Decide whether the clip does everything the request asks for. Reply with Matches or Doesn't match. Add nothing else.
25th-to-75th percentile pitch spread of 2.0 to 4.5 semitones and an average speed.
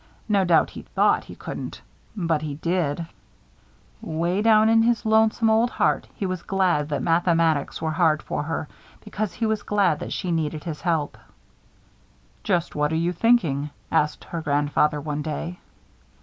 Doesn't match